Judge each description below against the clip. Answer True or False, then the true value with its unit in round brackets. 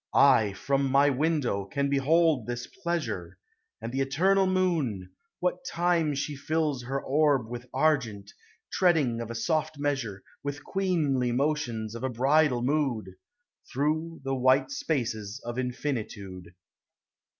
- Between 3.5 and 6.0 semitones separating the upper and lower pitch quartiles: True (4.6 semitones)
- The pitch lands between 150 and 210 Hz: False (135 Hz)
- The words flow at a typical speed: False (130 wpm)